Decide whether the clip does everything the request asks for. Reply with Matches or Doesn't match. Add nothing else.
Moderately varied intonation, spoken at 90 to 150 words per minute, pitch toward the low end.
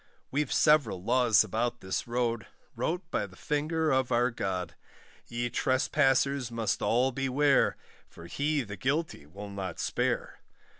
Matches